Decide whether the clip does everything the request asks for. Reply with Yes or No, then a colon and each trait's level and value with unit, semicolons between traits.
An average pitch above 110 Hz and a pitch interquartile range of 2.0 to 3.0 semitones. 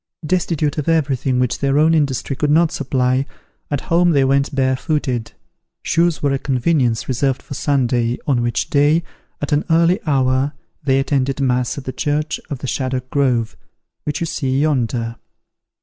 Yes: medium, 140 Hz; average, 2.7 semitones